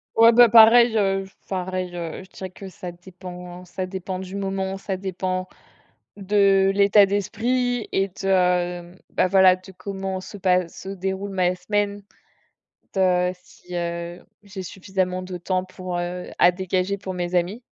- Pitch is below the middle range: No, high, 190 Hz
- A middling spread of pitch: No, narrow, 1.5 semitones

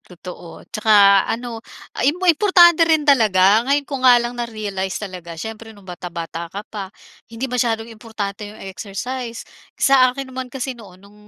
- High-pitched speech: Yes, high, 225 Hz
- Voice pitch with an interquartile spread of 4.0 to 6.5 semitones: Yes, average, 4.4 semitones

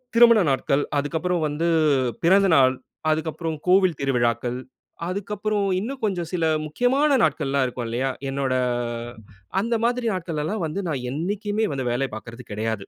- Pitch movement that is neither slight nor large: No, wide, 7.2 semitones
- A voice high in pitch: No, medium, 160 Hz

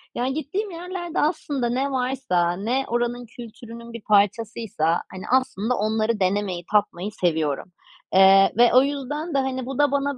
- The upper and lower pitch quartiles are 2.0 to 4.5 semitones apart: No, average, 4.9 semitones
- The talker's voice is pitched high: Yes, high, 235 Hz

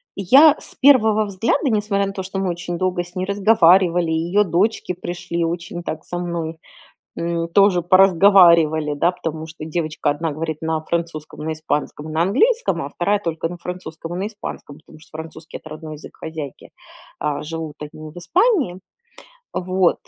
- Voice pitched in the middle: Yes, medium, 170 Hz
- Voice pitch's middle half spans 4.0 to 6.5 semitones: No, average, 3.3 semitones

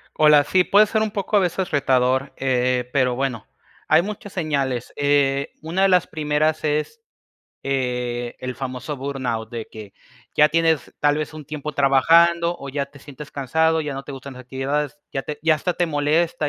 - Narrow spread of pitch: No, average, 3.3 semitones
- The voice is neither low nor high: Yes, medium, 145 Hz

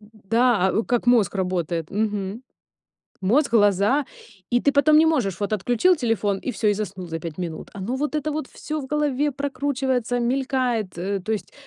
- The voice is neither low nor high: No, high, 230 Hz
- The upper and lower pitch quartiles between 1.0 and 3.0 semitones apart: No, wide, 5.4 semitones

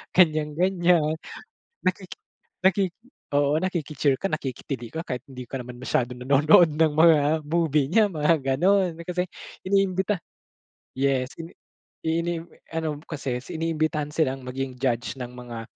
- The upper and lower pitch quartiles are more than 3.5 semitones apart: Yes, average, 4.4 semitones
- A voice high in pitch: No, medium, 150 Hz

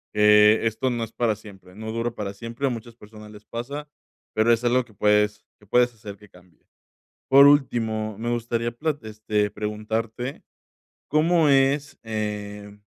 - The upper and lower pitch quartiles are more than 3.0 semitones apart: No, narrow, 2.5 semitones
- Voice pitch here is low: Yes, low, 110 Hz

